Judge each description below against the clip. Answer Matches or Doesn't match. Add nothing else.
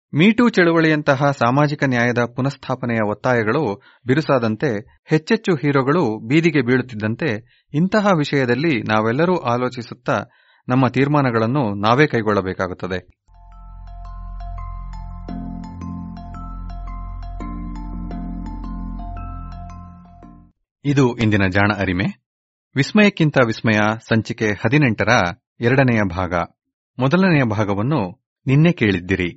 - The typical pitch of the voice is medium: Doesn't match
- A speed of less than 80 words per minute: Matches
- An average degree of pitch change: Doesn't match